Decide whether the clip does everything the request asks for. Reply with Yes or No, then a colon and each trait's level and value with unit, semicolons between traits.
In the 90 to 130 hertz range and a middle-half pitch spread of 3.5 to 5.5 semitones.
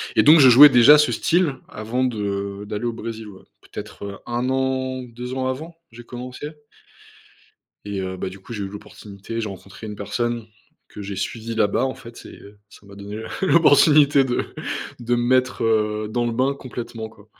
Yes: low, 115 Hz; average, 3.8 semitones